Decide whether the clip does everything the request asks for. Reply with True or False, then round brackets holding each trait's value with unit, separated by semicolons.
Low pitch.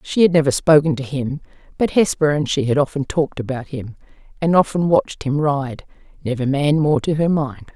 False (145 Hz)